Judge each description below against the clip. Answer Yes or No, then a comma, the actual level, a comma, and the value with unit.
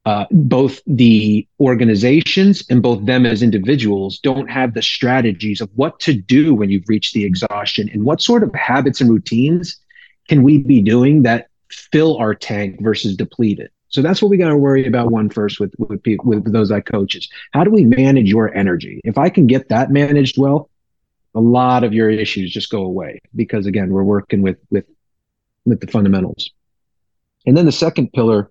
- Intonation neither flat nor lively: Yes, average, 4.6 semitones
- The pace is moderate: Yes, average, 195 wpm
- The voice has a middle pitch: No, low, 115 Hz